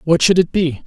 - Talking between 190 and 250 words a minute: No, fast, 275 wpm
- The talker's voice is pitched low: No, medium, 170 Hz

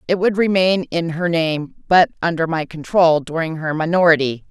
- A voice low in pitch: No, medium, 165 Hz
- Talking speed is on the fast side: No, average, 175 wpm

